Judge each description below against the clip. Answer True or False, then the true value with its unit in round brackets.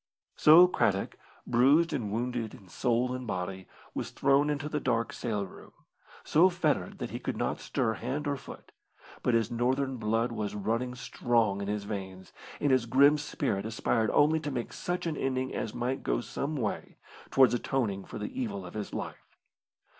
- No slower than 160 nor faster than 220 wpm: True (180 wpm)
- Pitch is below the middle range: True (125 Hz)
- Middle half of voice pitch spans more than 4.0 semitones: True (4.8 semitones)